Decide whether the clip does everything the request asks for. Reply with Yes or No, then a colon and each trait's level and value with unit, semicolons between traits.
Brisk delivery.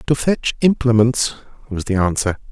No: average, 145 wpm